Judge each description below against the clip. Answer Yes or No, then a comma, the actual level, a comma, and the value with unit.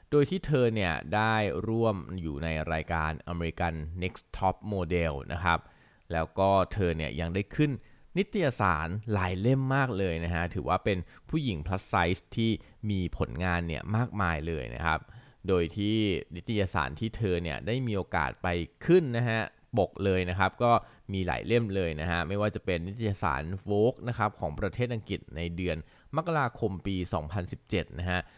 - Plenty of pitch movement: No, average, 4.6 semitones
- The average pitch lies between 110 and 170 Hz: No, very low, 95 Hz